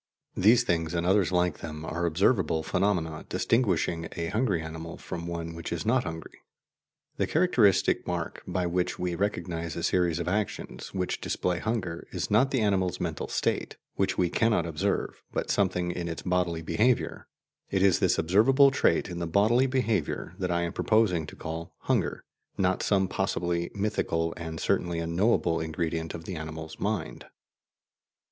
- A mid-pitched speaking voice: No, very low, 90 Hz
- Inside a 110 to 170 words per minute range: Yes, average, 165 wpm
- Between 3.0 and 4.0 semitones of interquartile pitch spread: Yes, average, 3.4 semitones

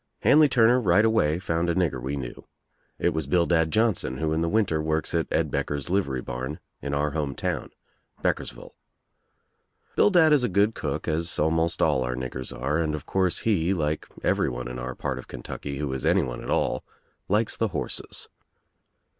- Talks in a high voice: No, very low, 80 Hz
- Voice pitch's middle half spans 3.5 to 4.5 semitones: No, wide, 5.4 semitones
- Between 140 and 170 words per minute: No, average, 180 wpm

